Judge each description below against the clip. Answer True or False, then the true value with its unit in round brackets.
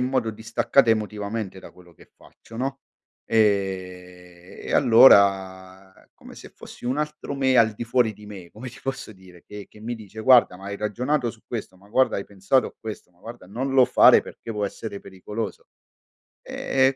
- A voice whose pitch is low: True (110 Hz)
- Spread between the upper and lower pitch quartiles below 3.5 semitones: False (4.1 semitones)